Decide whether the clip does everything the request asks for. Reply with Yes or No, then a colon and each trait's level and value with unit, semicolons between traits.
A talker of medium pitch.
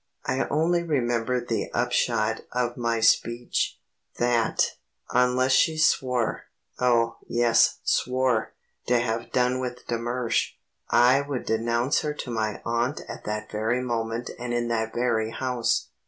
No: low, 120 Hz